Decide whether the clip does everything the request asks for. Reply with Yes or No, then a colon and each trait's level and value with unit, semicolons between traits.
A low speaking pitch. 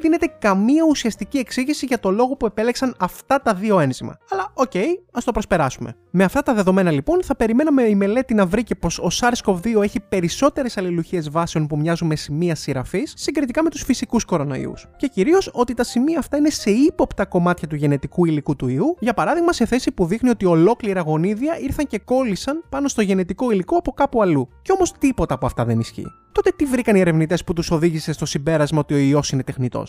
No: high, 205 Hz